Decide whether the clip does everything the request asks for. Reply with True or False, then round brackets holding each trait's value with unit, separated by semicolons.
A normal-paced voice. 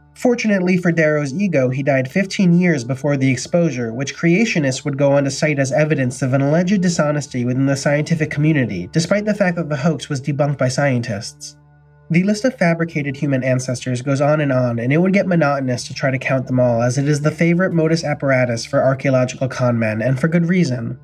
False (210 wpm)